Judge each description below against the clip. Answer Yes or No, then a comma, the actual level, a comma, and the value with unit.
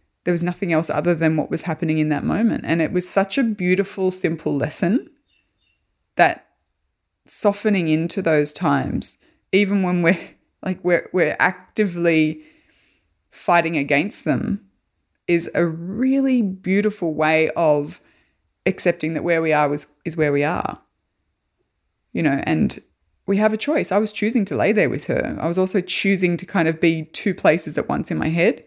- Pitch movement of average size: Yes, average, 4.0 semitones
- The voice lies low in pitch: No, medium, 175 Hz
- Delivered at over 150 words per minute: Yes, average, 170 wpm